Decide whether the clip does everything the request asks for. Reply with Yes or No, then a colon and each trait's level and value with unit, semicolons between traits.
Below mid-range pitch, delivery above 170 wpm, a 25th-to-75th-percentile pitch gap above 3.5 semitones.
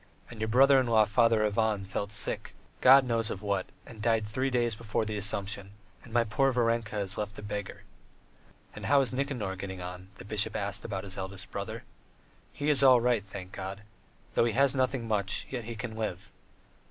No: low, 110 Hz; average, 200 wpm; average, 3.2 semitones